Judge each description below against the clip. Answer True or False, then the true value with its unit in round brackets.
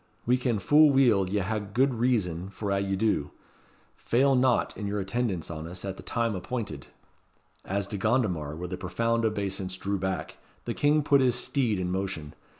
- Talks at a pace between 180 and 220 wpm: True (185 wpm)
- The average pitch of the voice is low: True (100 Hz)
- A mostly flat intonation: False (4.6 semitones)